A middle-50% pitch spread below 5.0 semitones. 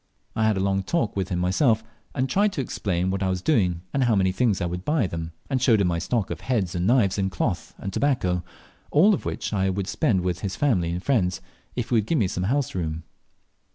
No: wide, 5.4 semitones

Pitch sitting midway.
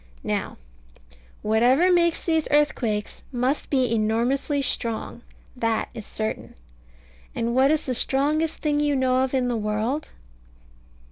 No: very high, 260 Hz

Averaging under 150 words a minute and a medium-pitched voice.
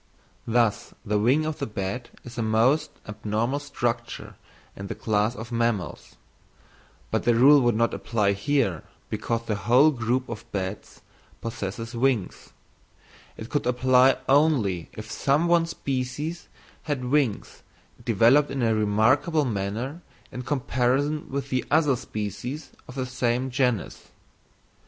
No: slow, 135 wpm; low, 120 Hz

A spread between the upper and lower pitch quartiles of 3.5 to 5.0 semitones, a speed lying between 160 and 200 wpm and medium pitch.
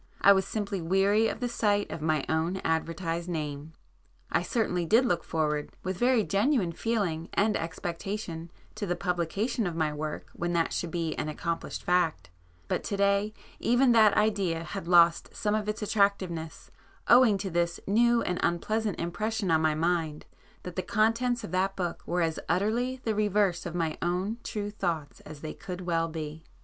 Yes: average, 4.2 semitones; average, 175 wpm; medium, 180 Hz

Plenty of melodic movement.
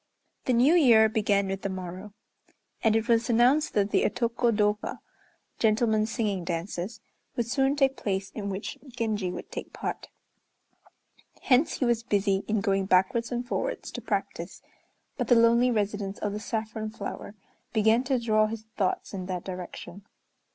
No: average, 3.0 semitones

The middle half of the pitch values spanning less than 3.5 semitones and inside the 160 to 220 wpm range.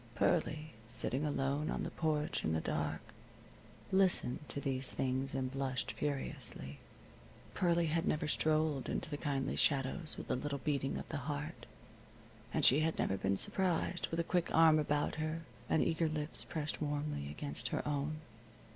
Yes: average, 2.7 semitones; average, 165 wpm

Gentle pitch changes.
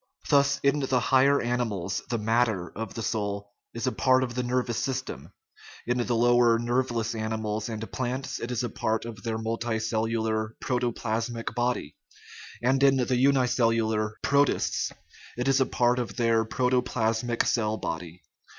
Yes: narrow, 2.1 semitones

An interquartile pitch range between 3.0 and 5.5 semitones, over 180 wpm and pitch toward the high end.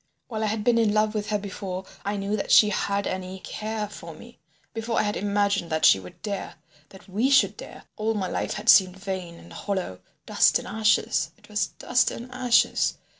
No: narrow, 2.5 semitones; fast, 205 wpm; high, 205 Hz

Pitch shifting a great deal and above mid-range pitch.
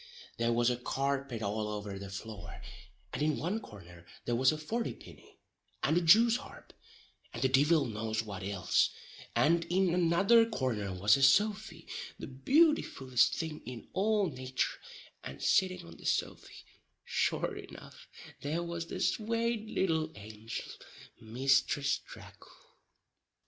No: wide, 8.0 semitones; low, 135 Hz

